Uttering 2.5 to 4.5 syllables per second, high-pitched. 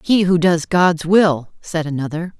No: 4.1 syllables/s; medium, 170 Hz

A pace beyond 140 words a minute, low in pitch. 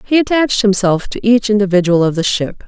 No: average, 200 wpm; high, 205 Hz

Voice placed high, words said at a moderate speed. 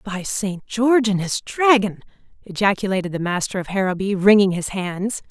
Yes: high, 200 Hz; average, 160 wpm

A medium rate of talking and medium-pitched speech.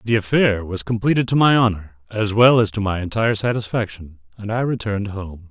No: average, 195 wpm; low, 105 Hz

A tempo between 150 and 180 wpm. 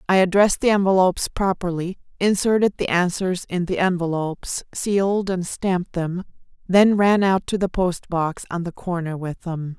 Yes: average, 165 wpm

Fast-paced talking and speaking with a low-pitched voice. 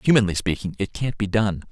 Yes: fast, 210 wpm; low, 100 Hz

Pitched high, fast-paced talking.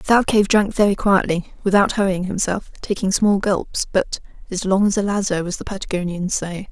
No: high, 195 Hz; average, 180 wpm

